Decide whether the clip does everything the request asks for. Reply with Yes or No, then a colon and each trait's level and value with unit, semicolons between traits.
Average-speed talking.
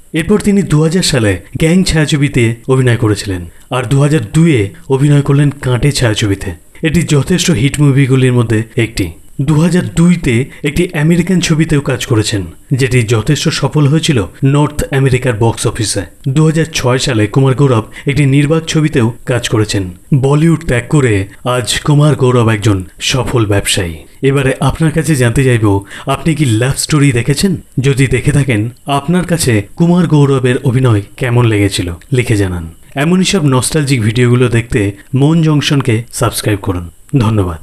No: fast, 140 wpm